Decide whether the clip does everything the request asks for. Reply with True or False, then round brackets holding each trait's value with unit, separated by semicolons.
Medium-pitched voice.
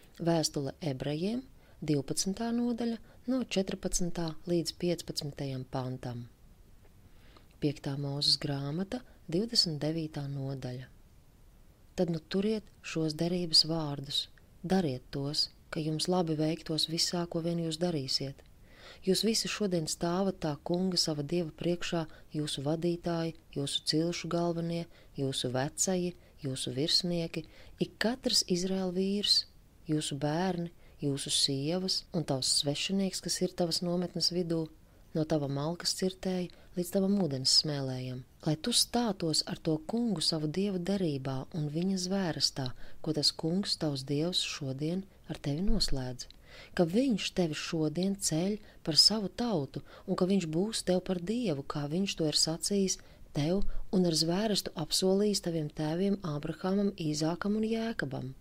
True (165 Hz)